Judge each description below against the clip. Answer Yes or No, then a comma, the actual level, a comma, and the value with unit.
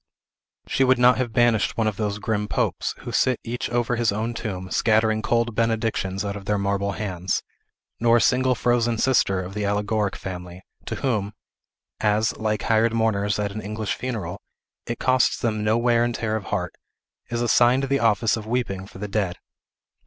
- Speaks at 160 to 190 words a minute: Yes, average, 185 wpm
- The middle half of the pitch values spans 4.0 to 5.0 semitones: No, average, 2.7 semitones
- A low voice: Yes, low, 110 Hz